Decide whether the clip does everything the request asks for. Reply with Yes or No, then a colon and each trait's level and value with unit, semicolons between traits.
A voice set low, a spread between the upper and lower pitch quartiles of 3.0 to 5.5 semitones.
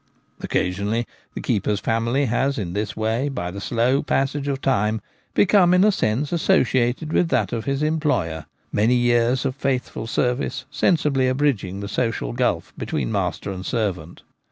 Yes: low, 120 Hz; average, 5.0 semitones